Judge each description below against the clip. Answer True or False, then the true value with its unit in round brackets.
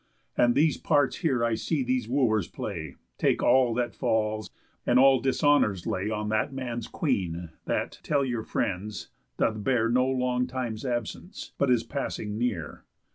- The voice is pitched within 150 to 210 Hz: False (120 Hz)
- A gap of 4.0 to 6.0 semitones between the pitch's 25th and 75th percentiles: False (3.4 semitones)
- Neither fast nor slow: True (160 wpm)